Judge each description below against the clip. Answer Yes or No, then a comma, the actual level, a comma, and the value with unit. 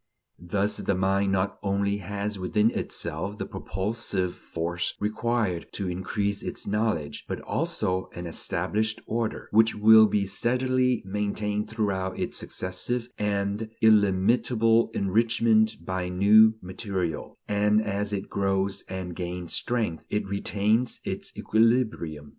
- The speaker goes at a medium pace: No, slow, 125 wpm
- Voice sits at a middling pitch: No, low, 100 Hz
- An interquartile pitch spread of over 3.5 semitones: No, average, 2.8 semitones